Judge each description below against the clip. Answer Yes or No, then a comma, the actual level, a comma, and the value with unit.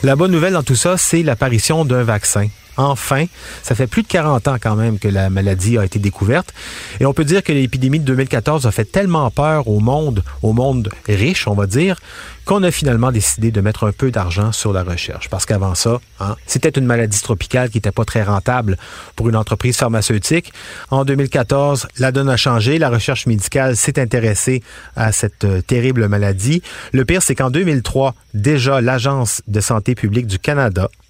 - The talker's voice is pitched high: No, low, 125 Hz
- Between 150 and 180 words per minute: No, average, 195 wpm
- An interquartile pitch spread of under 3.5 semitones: No, average, 4.5 semitones